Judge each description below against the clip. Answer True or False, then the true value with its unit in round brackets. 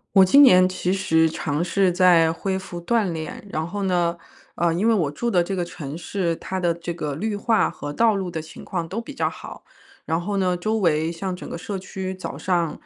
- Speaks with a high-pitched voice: False (180 Hz)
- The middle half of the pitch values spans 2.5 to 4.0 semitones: True (2.8 semitones)